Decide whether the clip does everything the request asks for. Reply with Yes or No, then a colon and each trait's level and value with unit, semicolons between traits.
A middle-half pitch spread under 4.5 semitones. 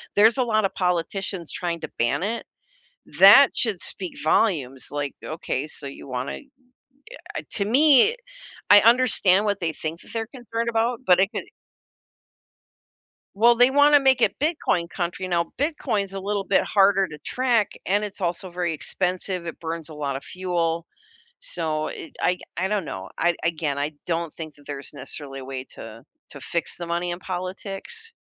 No: average, 5.1 semitones